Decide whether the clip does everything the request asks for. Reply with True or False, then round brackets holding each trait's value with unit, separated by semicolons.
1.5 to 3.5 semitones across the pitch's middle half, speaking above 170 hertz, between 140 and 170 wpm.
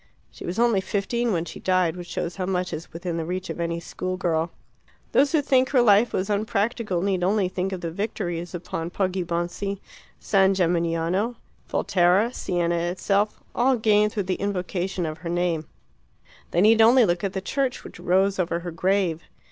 False (3.1 semitones; 185 Hz; 180 wpm)